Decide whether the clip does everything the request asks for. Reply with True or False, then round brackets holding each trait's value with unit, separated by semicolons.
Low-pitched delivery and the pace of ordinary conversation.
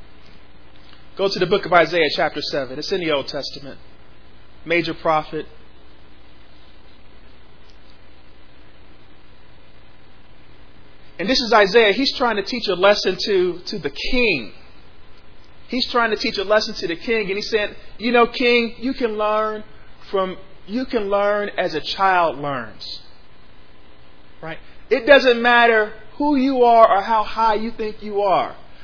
False (185 Hz; 145 wpm)